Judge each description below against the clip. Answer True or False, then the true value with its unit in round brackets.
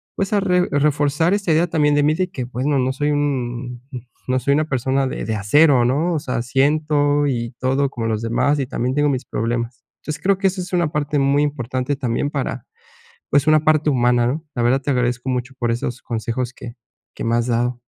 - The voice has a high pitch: False (135 Hz)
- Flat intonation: False (3.5 semitones)